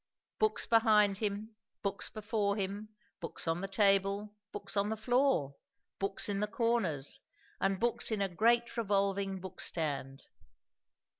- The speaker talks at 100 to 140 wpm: Yes, slow, 135 wpm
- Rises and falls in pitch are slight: Yes, narrow, 2.0 semitones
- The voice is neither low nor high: No, high, 200 Hz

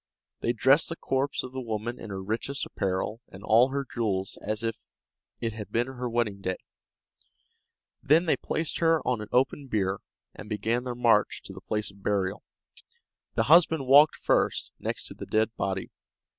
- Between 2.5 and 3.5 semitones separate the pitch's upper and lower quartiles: No, average, 4.1 semitones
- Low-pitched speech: Yes, low, 115 Hz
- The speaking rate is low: No, average, 180 wpm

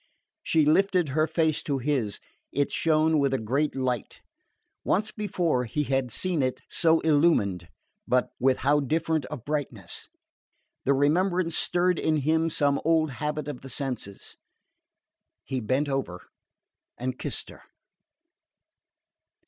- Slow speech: Yes, slow, 130 wpm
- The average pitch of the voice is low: No, medium, 145 Hz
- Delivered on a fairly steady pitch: No, average, 3.6 semitones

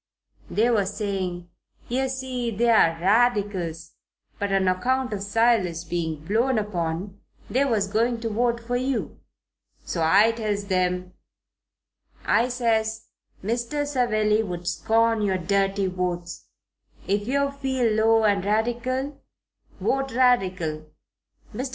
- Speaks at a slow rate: Yes, slow, 125 wpm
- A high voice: Yes, high, 215 Hz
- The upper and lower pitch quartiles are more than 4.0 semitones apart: Yes, average, 4.4 semitones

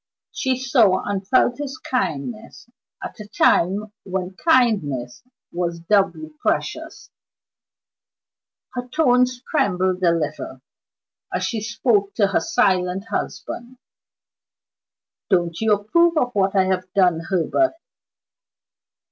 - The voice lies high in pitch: Yes, high, 200 Hz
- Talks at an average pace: No, slow, 110 wpm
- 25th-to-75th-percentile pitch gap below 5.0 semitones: No, average, 5.3 semitones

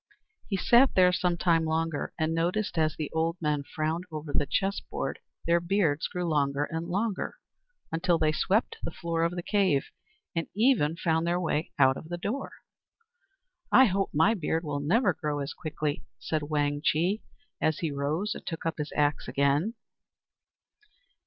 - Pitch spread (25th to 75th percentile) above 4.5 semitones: No, average, 3.2 semitones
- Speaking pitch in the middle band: Yes, medium, 165 Hz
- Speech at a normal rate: Yes, average, 170 wpm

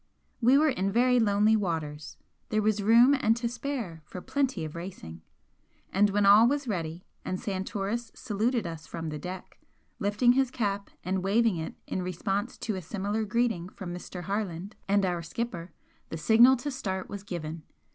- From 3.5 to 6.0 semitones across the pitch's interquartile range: Yes, average, 4.6 semitones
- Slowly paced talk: No, average, 175 wpm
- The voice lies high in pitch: Yes, high, 200 Hz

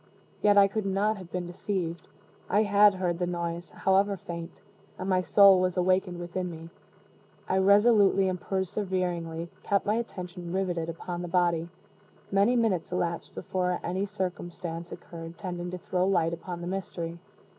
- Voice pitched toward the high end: No, medium, 180 Hz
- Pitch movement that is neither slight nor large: No, narrow, 2.1 semitones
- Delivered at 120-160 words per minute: Yes, average, 155 wpm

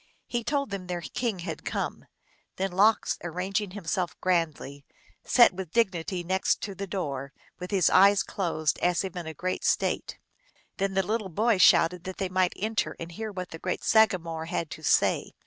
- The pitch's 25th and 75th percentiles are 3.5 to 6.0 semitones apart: No, narrow, 2.6 semitones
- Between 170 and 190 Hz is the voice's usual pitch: Yes, medium, 185 Hz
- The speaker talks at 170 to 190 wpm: Yes, average, 175 wpm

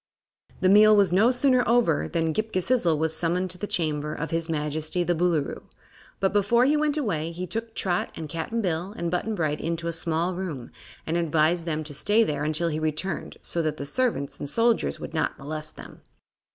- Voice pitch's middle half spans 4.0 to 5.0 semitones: Yes, average, 4.7 semitones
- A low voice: No, medium, 170 Hz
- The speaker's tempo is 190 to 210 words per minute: Yes, fast, 205 wpm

